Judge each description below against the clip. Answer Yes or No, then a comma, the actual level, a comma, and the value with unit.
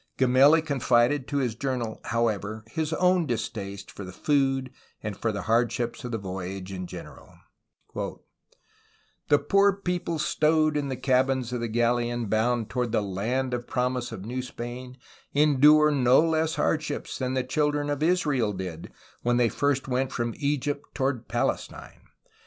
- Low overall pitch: Yes, low, 125 Hz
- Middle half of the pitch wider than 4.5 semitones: No, average, 4.1 semitones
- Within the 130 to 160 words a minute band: Yes, average, 150 wpm